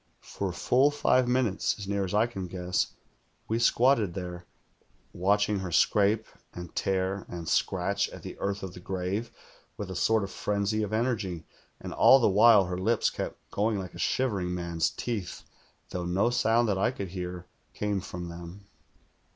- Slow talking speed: No, average, 175 wpm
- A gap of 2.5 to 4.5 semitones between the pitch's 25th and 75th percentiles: Yes, average, 3.4 semitones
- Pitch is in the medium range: No, low, 100 Hz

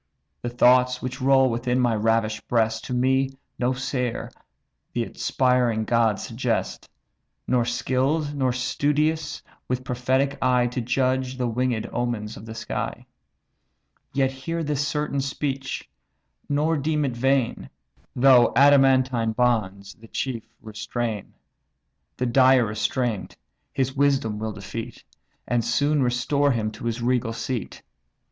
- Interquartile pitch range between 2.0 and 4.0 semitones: Yes, narrow, 2.6 semitones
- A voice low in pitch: Yes, low, 125 Hz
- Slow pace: Yes, slow, 130 wpm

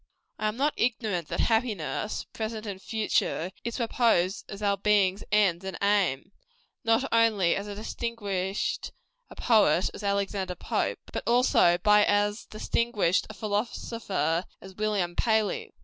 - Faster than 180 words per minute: No, average, 140 wpm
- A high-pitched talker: Yes, high, 205 Hz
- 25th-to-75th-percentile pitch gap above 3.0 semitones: No, average, 2.7 semitones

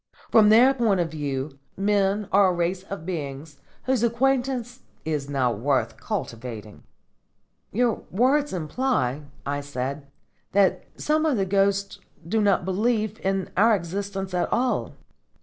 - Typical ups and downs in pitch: No, wide, 7.2 semitones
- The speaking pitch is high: Yes, high, 195 Hz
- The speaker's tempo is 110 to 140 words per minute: Yes, slow, 135 wpm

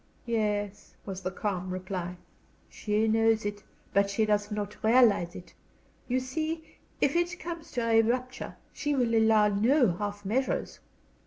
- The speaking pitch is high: Yes, high, 220 Hz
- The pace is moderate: Yes, average, 150 wpm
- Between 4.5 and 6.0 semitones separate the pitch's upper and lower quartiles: No, average, 3.8 semitones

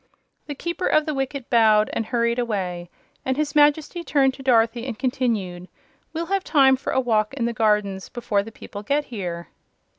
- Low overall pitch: No, high, 240 Hz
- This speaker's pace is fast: No, average, 185 wpm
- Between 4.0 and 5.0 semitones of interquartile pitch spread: Yes, average, 4.7 semitones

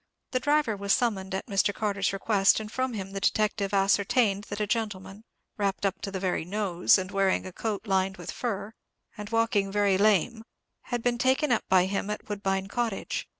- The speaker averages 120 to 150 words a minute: No, average, 195 wpm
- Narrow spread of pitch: Yes, narrow, 2.3 semitones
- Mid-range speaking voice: No, high, 200 Hz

